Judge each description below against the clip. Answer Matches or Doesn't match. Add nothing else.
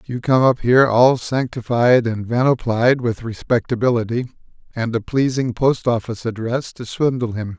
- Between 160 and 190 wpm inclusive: Doesn't match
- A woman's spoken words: Doesn't match